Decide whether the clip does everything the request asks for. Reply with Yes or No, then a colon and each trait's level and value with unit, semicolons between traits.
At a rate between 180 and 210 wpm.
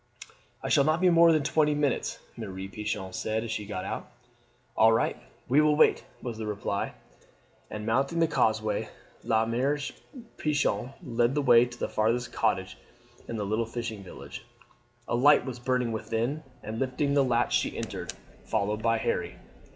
No: average, 170 wpm